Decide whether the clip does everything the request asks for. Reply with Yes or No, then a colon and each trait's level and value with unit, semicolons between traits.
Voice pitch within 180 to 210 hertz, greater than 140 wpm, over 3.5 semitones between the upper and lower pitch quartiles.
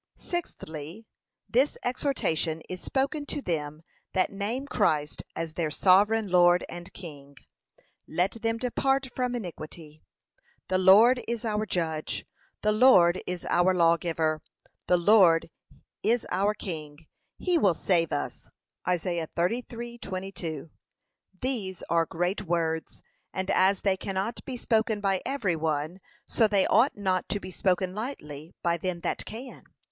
No: medium, 185 Hz; slow, 135 wpm; average, 5.1 semitones